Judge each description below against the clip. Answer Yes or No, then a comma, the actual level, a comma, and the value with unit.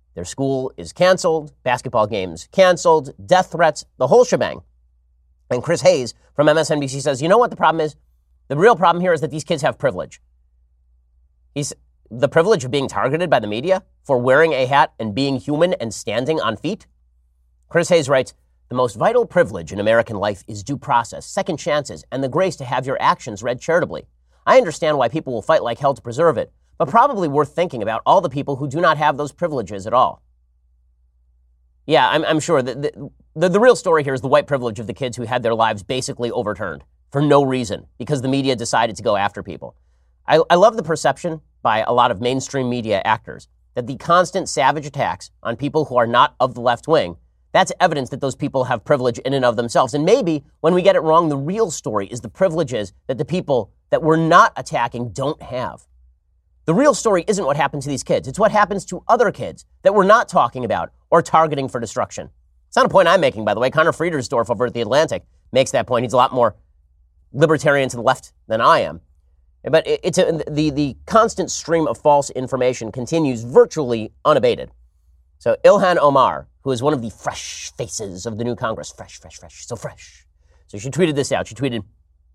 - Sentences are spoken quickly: Yes, fast, 210 wpm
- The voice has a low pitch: Yes, low, 130 Hz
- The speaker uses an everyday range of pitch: No, wide, 8.6 semitones